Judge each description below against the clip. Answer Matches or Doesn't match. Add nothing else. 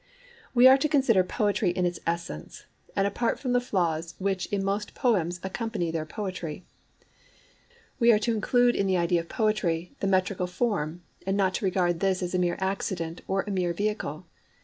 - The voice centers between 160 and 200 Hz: Matches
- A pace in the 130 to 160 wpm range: Doesn't match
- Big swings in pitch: Doesn't match